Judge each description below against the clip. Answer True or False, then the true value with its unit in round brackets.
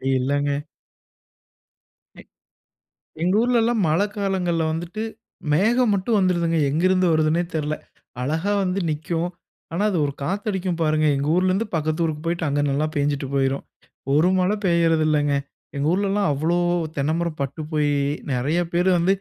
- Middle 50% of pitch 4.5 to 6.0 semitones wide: False (3.8 semitones)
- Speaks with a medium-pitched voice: True (170 Hz)